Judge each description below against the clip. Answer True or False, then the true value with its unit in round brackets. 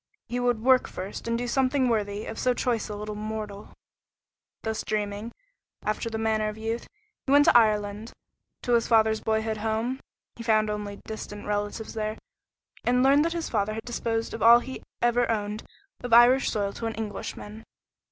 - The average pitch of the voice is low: False (220 Hz)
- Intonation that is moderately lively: False (2.2 semitones)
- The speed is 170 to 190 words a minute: True (180 wpm)